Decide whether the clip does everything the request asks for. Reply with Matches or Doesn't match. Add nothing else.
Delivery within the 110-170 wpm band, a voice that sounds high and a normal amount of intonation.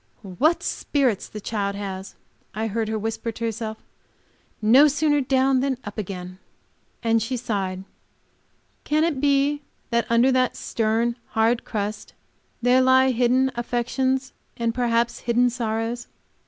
Matches